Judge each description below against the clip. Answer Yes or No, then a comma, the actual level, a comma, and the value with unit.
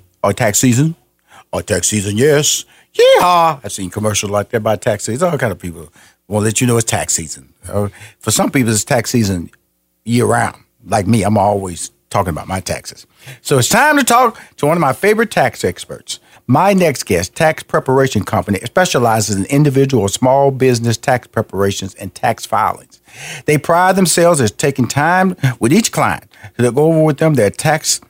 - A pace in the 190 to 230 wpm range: Yes, average, 195 wpm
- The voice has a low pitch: Yes, low, 120 Hz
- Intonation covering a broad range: Yes, wide, 6.5 semitones